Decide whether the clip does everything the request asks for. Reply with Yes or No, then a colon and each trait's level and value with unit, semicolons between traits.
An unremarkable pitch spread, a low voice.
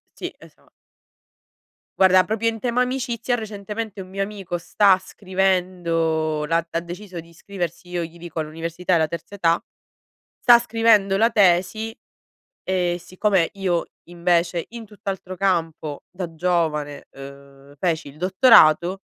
No: average, 3.3 semitones; medium, 180 Hz